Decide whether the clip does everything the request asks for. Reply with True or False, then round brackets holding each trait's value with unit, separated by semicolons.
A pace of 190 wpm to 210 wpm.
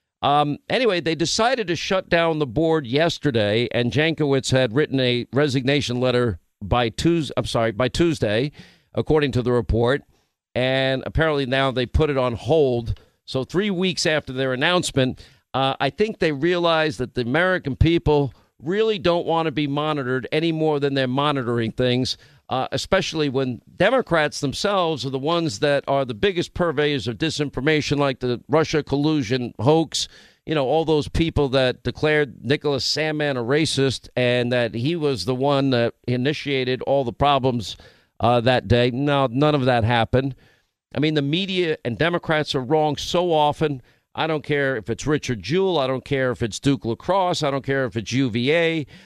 False (175 wpm)